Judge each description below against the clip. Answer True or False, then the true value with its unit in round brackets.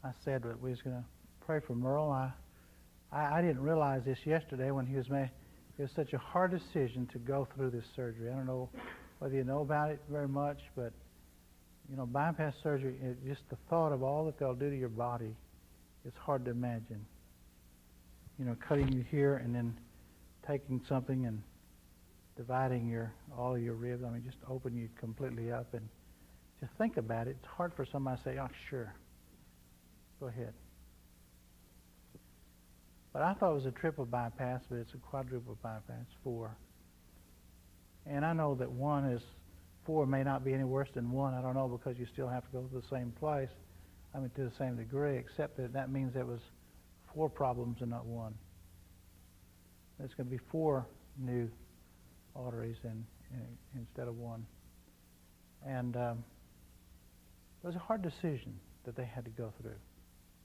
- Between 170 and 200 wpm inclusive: True (185 wpm)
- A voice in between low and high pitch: False (125 Hz)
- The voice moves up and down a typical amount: False (7.3 semitones)